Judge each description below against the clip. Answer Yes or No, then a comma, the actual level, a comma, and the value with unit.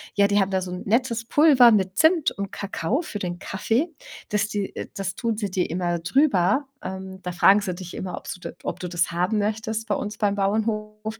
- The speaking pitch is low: No, high, 205 Hz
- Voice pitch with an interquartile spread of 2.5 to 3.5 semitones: Yes, average, 3.0 semitones